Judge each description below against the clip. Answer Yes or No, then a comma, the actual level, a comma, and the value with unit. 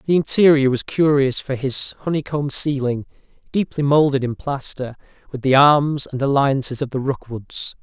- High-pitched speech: No, medium, 140 Hz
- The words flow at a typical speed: Yes, average, 155 wpm